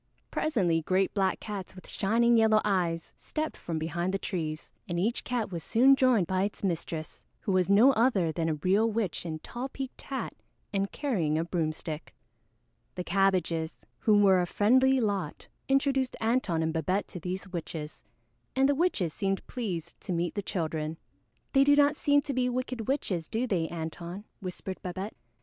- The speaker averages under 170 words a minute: No, average, 175 wpm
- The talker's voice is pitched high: Yes, high, 195 Hz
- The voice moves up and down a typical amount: No, wide, 5.9 semitones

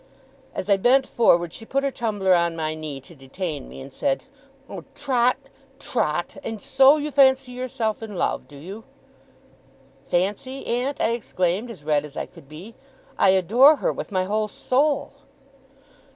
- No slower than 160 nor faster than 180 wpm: Yes, average, 165 wpm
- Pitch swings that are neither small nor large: No, wide, 7.0 semitones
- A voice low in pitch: No, high, 215 Hz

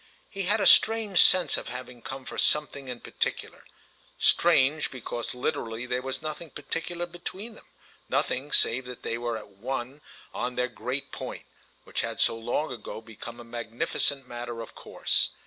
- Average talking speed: Yes, average, 165 wpm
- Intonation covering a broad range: No, average, 4.5 semitones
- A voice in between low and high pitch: No, low, 125 Hz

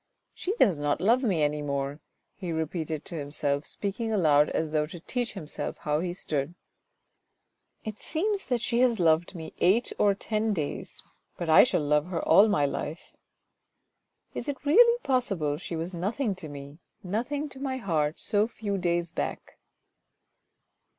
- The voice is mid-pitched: Yes, medium, 175 Hz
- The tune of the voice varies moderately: No, wide, 6.8 semitones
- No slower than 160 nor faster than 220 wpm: Yes, average, 170 wpm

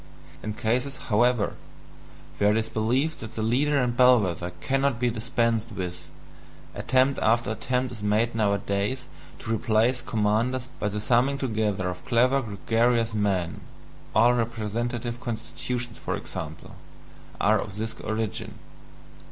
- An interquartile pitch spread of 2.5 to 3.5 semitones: Yes, average, 2.8 semitones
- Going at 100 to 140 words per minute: Yes, slow, 135 wpm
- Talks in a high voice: No, low, 115 Hz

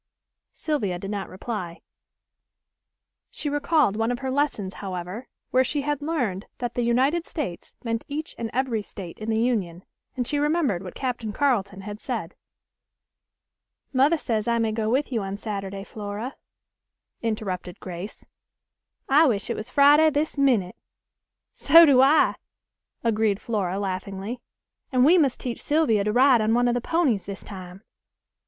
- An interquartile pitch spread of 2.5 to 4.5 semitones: No, wide, 5.6 semitones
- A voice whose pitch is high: Yes, high, 230 Hz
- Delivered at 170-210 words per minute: No, average, 155 wpm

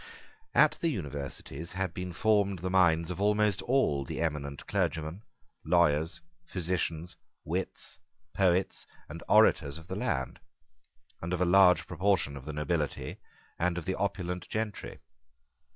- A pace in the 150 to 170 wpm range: No, slow, 135 wpm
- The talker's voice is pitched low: Yes, very low, 90 Hz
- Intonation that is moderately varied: Yes, average, 3.3 semitones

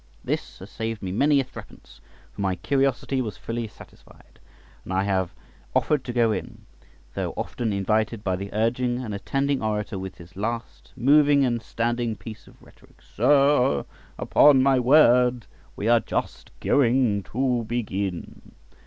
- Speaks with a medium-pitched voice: No, low, 115 Hz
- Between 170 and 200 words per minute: No, average, 155 wpm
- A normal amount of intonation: Yes, average, 4.2 semitones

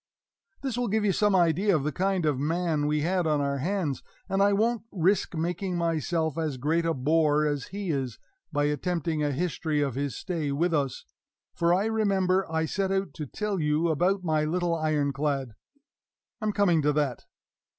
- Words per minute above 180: Yes, average, 190 wpm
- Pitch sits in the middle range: Yes, medium, 165 Hz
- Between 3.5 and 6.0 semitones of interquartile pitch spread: Yes, average, 4.3 semitones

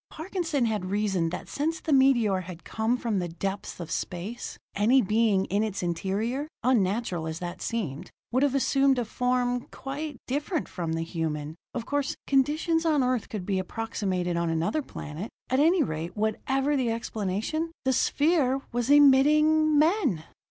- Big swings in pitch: Yes, wide, 7.0 semitones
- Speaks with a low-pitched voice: No, high, 235 Hz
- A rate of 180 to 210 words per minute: No, average, 160 wpm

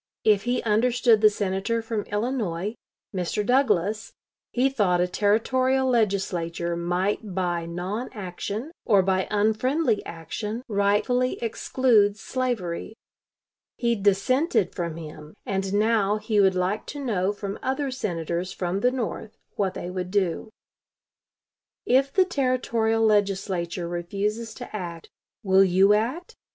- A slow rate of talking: Yes, slow, 125 wpm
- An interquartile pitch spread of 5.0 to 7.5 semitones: No, average, 4.1 semitones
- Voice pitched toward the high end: Yes, high, 205 Hz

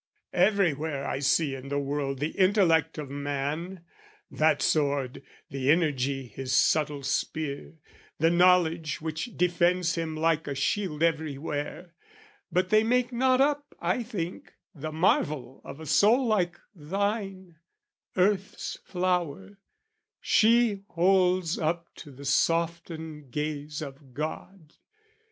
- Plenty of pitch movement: No, average, 4.2 semitones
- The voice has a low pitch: No, medium, 165 Hz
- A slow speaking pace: Yes, slow, 120 wpm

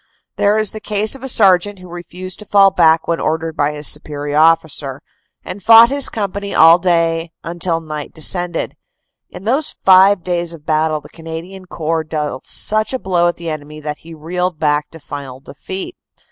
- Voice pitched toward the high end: No, medium, 170 Hz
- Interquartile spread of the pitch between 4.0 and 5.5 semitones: No, average, 3.6 semitones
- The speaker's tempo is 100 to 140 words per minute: No, average, 190 wpm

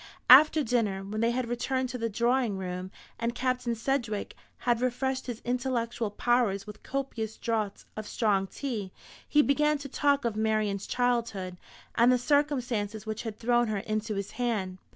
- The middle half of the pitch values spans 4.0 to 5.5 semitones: No, average, 3.0 semitones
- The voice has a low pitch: No, high, 235 Hz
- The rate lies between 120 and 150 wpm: No, average, 165 wpm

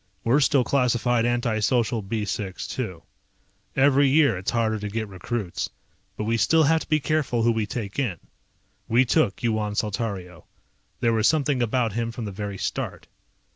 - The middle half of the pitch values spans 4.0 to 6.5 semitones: No, average, 3.4 semitones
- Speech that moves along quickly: No, average, 175 wpm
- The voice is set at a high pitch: No, low, 115 Hz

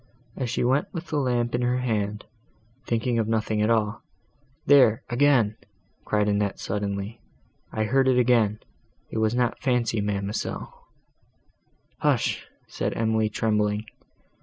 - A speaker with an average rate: No, slow, 120 wpm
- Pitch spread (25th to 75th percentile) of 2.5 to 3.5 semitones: Yes, average, 2.8 semitones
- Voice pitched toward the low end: Yes, low, 115 Hz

